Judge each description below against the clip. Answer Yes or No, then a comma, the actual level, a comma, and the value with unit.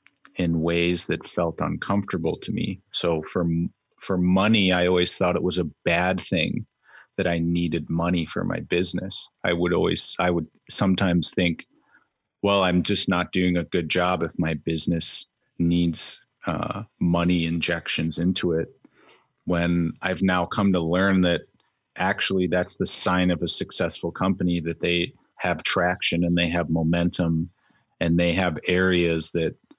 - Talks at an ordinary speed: Yes, average, 155 wpm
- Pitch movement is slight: Yes, narrow, 1.3 semitones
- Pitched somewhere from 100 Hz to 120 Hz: No, very low, 85 Hz